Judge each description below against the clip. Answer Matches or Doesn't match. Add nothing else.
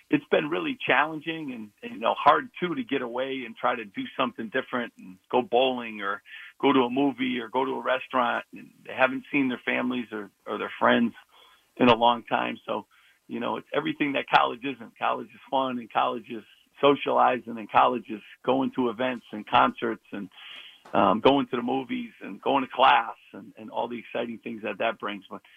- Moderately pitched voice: Doesn't match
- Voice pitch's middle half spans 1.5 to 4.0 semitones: Matches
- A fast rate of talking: Matches